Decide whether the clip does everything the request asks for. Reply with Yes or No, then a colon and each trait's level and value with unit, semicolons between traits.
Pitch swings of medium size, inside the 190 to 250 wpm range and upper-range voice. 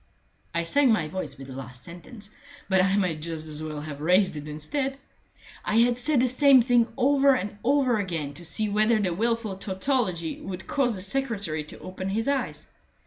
No: wide, 6.7 semitones; average, 195 wpm; high, 200 Hz